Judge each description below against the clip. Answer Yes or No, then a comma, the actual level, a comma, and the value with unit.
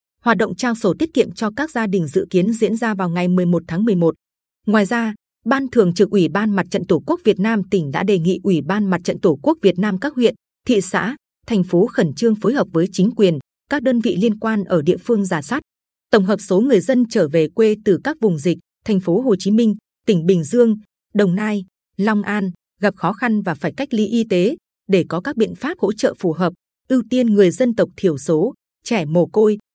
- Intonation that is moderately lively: Yes, average, 3.9 semitones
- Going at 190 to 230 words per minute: No, average, 240 wpm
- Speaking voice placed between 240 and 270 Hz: No, high, 205 Hz